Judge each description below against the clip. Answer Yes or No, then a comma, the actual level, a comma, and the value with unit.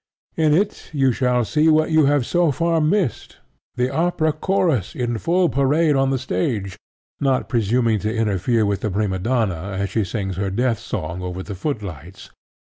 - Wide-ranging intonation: Yes, wide, 7.2 semitones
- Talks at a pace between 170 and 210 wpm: Yes, average, 175 wpm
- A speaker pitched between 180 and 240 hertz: No, low, 120 Hz